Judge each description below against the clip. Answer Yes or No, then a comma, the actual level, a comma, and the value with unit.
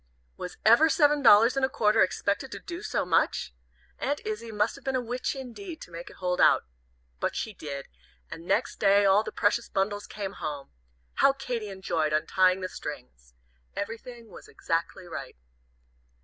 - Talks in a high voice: Yes, high, 205 Hz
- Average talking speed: Yes, average, 175 wpm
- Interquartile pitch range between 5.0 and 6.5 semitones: Yes, wide, 5.4 semitones